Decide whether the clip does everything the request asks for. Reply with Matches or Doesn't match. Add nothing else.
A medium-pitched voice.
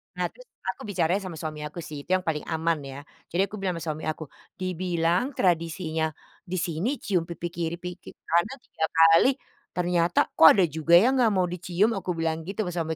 Matches